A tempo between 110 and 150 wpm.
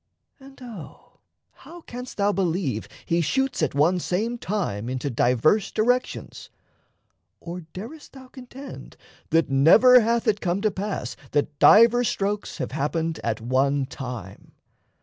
Yes: slow, 135 wpm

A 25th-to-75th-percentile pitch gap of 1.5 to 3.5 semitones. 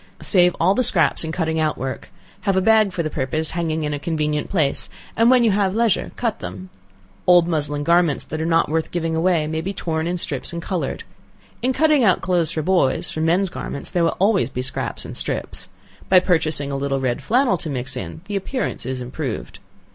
No: average, 4.1 semitones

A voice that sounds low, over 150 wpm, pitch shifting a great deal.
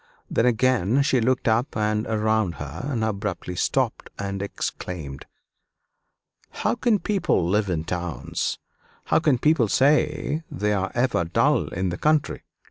No: low, 110 Hz; average, 140 wpm; wide, 6.1 semitones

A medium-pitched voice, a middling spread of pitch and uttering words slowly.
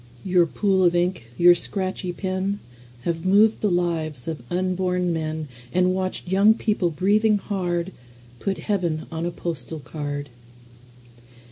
Yes: medium, 175 Hz; average, 3.2 semitones; slow, 120 wpm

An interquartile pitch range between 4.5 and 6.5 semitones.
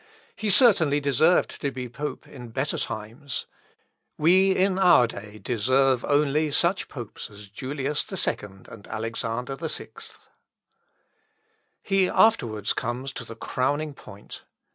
Yes: average, 5.2 semitones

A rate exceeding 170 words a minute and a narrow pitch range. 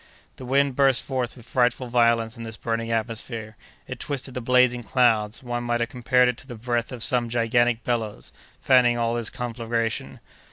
Yes: average, 185 wpm; narrow, 1.5 semitones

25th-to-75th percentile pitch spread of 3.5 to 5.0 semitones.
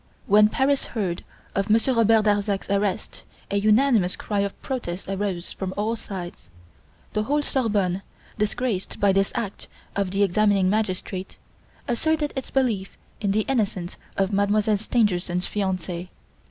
No: narrow, 2.6 semitones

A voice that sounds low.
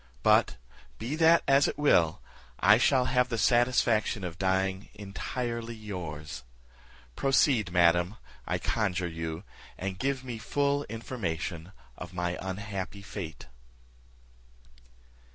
Yes: low, 105 Hz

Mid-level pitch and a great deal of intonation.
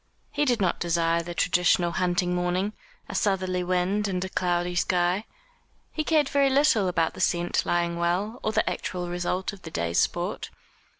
No: medium, 180 Hz; narrow, 2.6 semitones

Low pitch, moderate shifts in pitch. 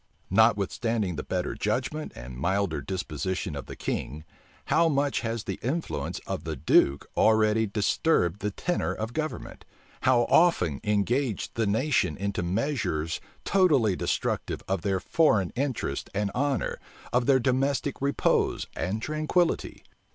No: low, 110 Hz; wide, 6.6 semitones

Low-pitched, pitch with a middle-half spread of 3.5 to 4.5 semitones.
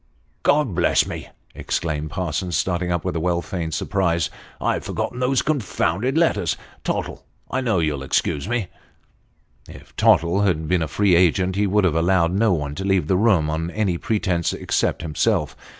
Yes: very low, 90 Hz; average, 4.0 semitones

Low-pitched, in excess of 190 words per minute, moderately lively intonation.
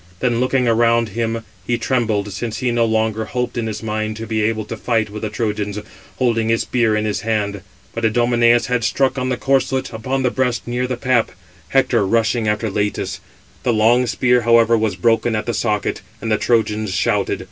No: low, 115 Hz; average, 200 wpm; narrow, 2.0 semitones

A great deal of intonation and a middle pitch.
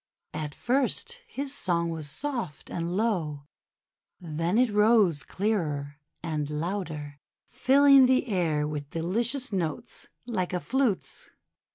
Yes: wide, 7.7 semitones; medium, 180 Hz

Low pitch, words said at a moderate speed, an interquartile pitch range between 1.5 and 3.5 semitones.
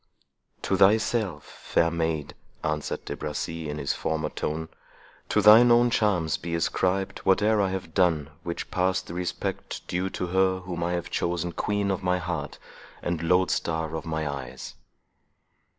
Yes: very low, 85 Hz; average, 150 wpm; average, 3.0 semitones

